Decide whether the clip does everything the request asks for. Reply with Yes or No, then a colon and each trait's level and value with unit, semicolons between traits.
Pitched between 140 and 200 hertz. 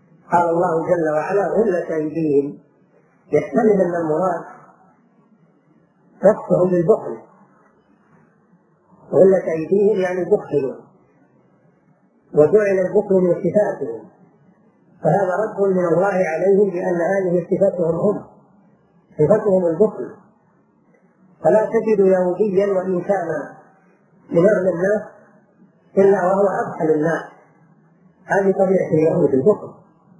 Yes: medium, 185 Hz